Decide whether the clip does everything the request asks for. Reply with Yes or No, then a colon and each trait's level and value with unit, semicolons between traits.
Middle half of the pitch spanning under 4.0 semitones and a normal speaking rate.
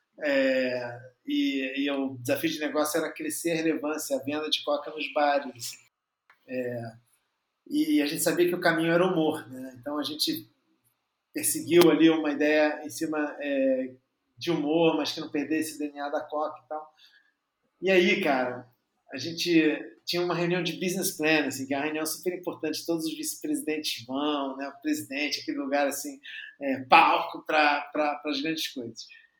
Yes: average, 3.4 semitones; average, 175 wpm